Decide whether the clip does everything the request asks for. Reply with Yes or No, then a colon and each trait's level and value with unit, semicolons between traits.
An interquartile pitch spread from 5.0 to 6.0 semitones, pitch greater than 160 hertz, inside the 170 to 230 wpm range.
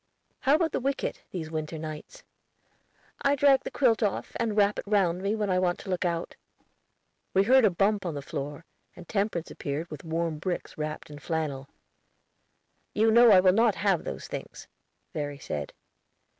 Yes: wide, 5.5 semitones; medium, 185 Hz; average, 185 wpm